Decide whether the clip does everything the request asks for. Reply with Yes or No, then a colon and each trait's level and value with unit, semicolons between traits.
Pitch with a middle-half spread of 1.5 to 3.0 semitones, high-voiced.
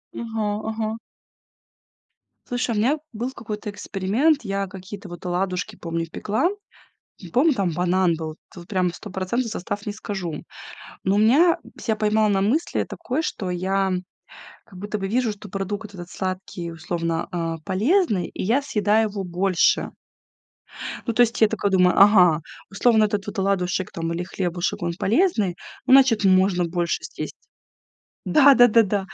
No: average, 3.4 semitones; high, 200 Hz